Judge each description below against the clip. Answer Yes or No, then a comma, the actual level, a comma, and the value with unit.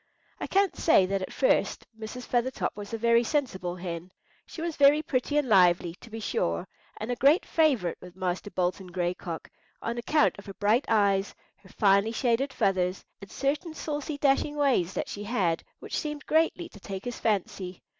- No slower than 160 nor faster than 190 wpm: Yes, average, 185 wpm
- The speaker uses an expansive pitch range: Yes, wide, 6.9 semitones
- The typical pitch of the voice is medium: No, high, 220 Hz